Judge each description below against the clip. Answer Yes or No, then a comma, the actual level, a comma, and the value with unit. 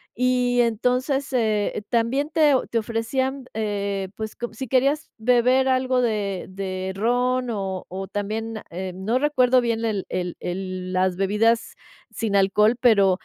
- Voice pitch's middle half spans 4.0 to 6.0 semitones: Yes, average, 4.3 semitones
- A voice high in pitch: Yes, high, 225 Hz